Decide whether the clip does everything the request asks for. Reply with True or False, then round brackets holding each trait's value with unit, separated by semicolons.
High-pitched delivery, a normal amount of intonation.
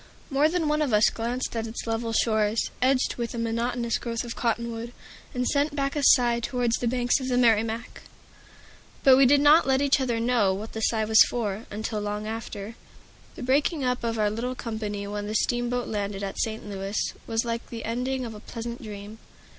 False (230 Hz; 2.3 semitones)